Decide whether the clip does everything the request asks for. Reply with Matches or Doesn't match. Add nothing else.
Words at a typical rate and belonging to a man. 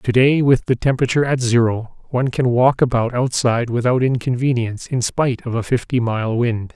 Matches